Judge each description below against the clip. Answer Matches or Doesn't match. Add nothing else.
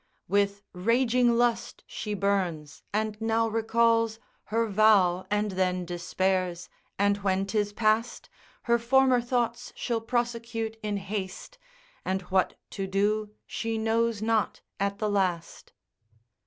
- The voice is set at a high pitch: Matches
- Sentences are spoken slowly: Matches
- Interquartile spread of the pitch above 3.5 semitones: Doesn't match